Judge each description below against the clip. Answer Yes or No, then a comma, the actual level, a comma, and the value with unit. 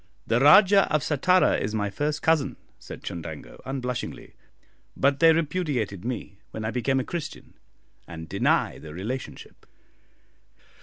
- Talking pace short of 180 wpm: Yes, slow, 135 wpm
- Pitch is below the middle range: Yes, low, 130 Hz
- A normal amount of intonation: No, wide, 6.3 semitones